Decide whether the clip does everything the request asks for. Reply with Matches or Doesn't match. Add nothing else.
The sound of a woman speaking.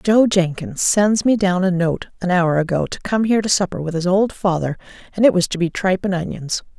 Matches